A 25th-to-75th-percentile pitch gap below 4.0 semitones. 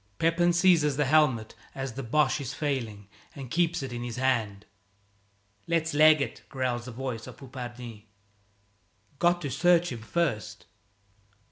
No: average, 4.5 semitones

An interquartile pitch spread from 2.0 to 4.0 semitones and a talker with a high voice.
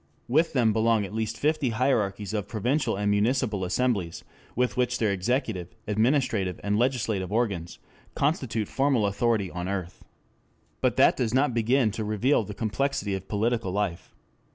No: average, 3.7 semitones; low, 110 Hz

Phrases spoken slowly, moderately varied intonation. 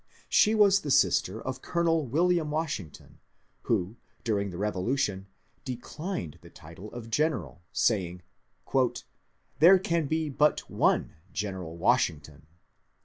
No: slow, 120 wpm; wide, 8.8 semitones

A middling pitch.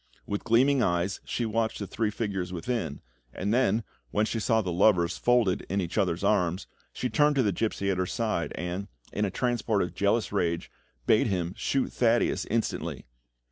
No: low, 100 Hz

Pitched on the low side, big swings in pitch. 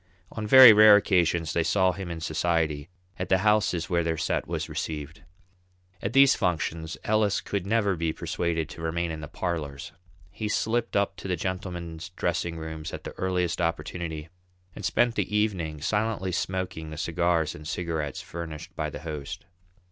No: very low, 85 Hz; average, 3.4 semitones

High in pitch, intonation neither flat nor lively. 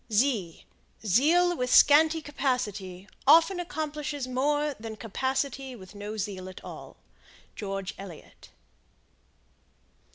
No: very high, 255 Hz; wide, 6.6 semitones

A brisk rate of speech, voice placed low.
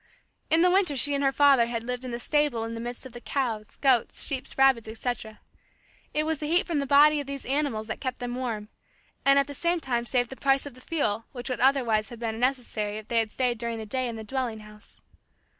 No: fast, 250 wpm; very high, 250 Hz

